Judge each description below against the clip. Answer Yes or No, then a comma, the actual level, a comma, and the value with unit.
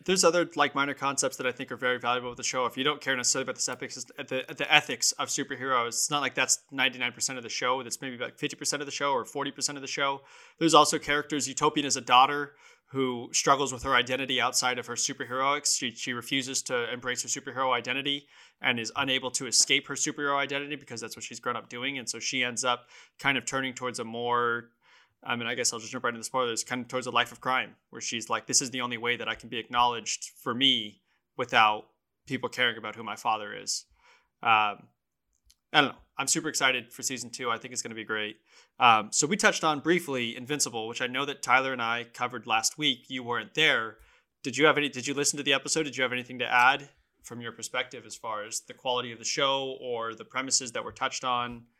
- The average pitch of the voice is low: Yes, low, 130 Hz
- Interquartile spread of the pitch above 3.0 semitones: No, narrow, 2.6 semitones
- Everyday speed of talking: No, fast, 240 wpm